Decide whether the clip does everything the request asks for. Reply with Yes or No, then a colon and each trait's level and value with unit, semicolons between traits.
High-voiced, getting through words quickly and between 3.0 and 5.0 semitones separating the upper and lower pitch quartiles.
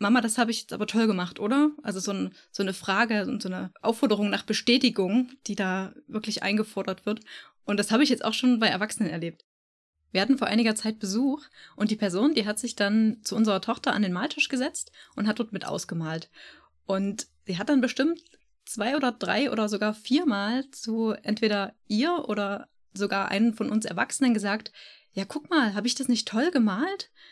Yes: high, 220 Hz; fast, 200 wpm; average, 3.8 semitones